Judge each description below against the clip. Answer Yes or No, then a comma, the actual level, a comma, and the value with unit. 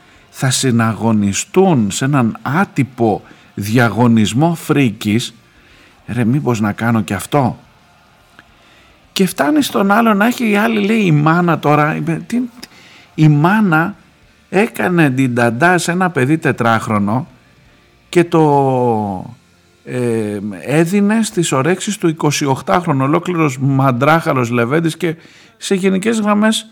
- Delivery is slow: Yes, slow, 110 wpm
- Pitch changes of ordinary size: No, wide, 7.4 semitones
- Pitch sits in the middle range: Yes, medium, 150 Hz